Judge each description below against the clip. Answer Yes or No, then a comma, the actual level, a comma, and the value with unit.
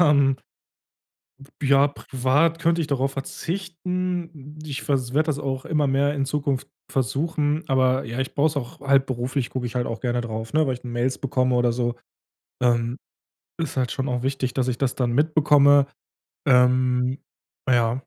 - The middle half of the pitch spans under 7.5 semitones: Yes, average, 2.7 semitones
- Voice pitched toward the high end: No, low, 135 Hz